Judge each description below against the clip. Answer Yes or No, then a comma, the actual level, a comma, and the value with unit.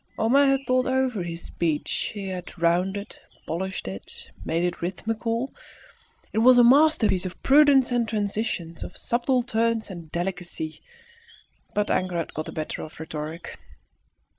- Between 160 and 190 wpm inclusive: No, average, 145 wpm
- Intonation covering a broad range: Yes, wide, 6.0 semitones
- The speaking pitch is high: Yes, high, 200 Hz